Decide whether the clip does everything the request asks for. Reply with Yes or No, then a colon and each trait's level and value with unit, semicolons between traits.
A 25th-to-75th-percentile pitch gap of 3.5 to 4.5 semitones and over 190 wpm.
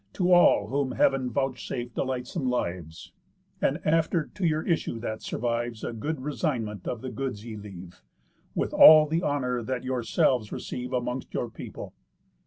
No: average, 3.8 semitones; average, 155 wpm